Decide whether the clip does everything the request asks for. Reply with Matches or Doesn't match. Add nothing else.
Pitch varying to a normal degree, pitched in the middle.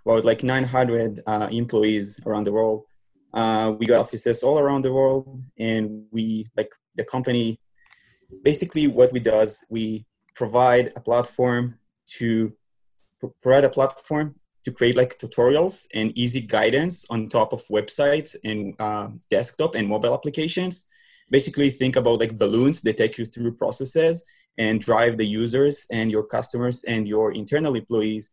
Doesn't match